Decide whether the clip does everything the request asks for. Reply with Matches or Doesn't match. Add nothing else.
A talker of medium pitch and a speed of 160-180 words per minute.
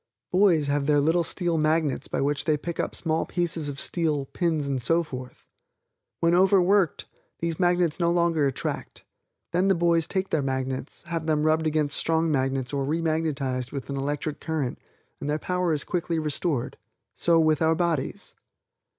Matches